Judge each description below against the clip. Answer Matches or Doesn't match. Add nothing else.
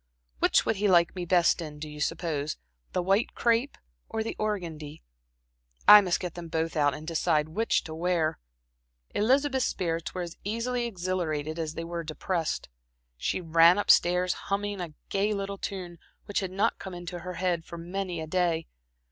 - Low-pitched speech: Doesn't match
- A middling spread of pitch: Matches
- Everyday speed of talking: Matches